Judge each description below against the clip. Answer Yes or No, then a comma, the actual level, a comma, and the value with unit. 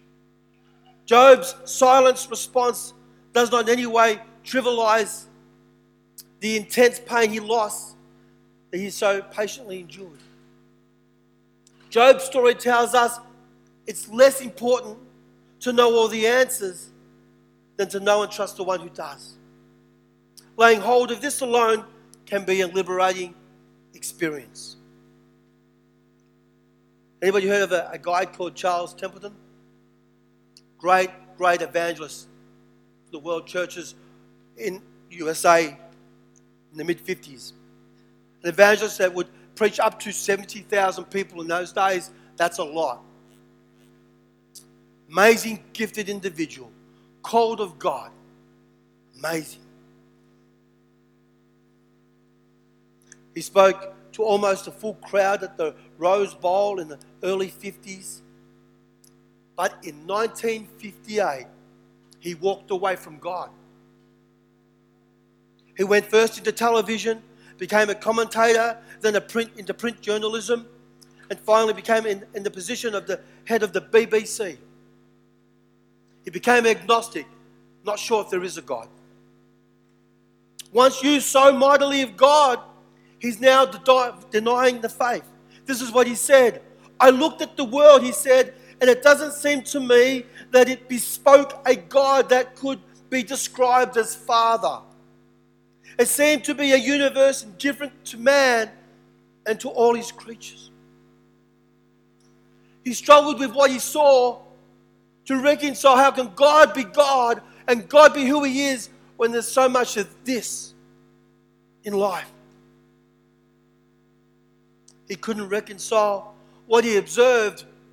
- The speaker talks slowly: Yes, slow, 120 wpm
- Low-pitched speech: No, high, 195 Hz